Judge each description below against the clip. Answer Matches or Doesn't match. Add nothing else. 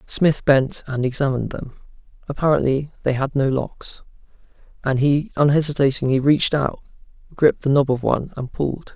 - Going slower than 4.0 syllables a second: Doesn't match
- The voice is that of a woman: Doesn't match